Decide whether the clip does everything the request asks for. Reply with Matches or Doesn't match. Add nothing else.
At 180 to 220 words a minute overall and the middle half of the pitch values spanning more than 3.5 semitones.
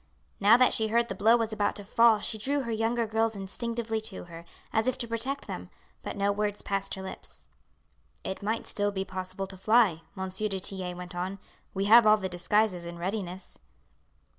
Doesn't match